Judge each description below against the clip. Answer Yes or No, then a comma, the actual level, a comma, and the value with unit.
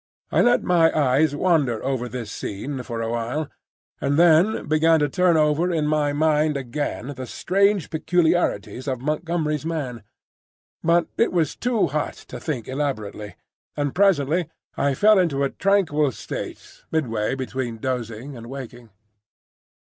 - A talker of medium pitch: Yes, medium, 145 Hz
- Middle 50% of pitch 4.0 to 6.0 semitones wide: Yes, average, 4.3 semitones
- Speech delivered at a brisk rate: No, average, 145 wpm